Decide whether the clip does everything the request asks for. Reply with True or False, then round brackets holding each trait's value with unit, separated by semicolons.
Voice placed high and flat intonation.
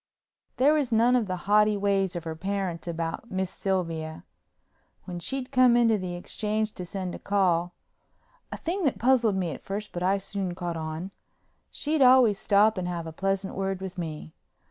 False (195 Hz; 3.7 semitones)